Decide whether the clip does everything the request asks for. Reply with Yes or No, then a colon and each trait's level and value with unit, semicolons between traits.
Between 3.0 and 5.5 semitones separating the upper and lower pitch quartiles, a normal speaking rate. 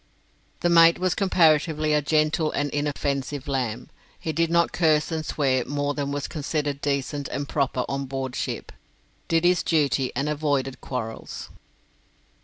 No: narrow, 2.4 semitones; average, 150 wpm